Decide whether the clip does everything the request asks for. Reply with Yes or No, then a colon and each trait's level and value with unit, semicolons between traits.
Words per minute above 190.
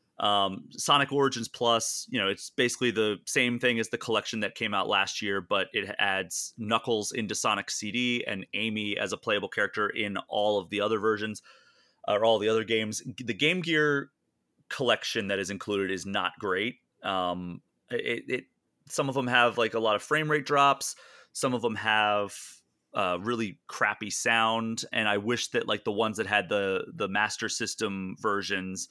No: average, 185 wpm